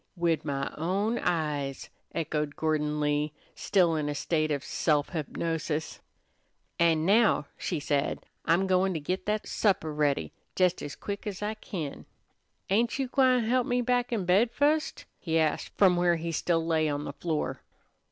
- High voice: No, medium, 170 Hz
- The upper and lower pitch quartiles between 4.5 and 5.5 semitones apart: Yes, average, 5.0 semitones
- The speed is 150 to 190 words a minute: Yes, average, 165 wpm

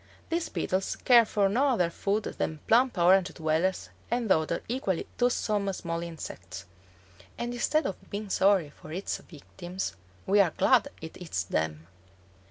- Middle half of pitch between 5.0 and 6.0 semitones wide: Yes, wide, 5.4 semitones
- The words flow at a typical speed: Yes, average, 150 wpm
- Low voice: No, high, 190 Hz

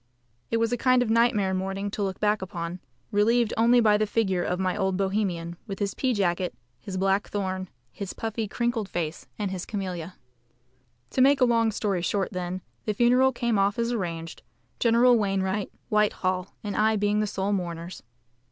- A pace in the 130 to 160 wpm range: No, average, 180 wpm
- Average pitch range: Yes, average, 3.2 semitones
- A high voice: Yes, high, 200 Hz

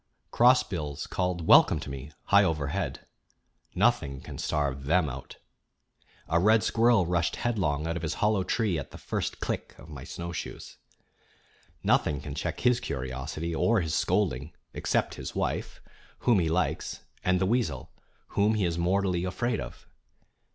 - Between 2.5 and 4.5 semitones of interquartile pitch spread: No, average, 5.3 semitones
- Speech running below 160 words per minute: Yes, average, 150 wpm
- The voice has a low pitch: Yes, very low, 85 Hz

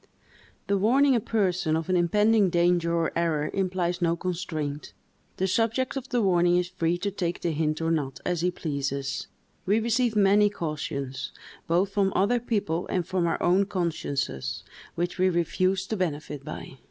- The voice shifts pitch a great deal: No, average, 3.4 semitones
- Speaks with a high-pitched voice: No, medium, 175 Hz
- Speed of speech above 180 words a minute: No, average, 170 wpm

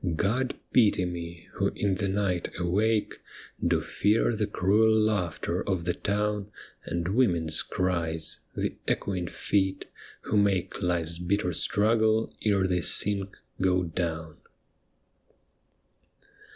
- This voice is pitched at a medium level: No, very low, 95 Hz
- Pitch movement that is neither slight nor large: Yes, average, 3.2 semitones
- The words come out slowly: Yes, slow, 120 wpm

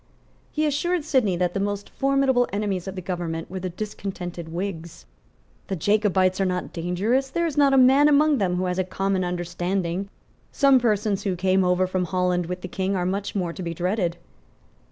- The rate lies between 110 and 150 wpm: No, average, 190 wpm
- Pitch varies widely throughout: No, average, 3.4 semitones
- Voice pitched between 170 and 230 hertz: Yes, high, 190 Hz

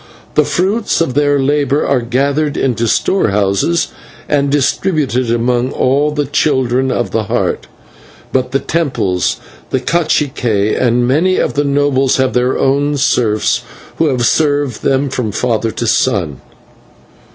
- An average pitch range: Yes, average, 3.3 semitones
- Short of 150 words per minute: Yes, average, 140 wpm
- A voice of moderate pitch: No, low, 130 Hz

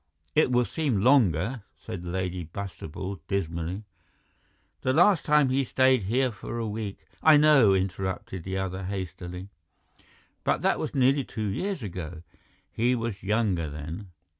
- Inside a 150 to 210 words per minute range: No, average, 140 wpm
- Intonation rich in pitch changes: Yes, wide, 5.8 semitones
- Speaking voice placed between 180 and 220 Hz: No, low, 100 Hz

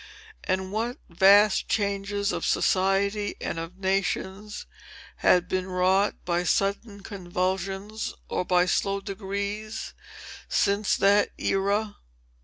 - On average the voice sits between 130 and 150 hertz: No, high, 195 Hz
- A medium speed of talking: No, slow, 105 wpm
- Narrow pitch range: Yes, narrow, 1.5 semitones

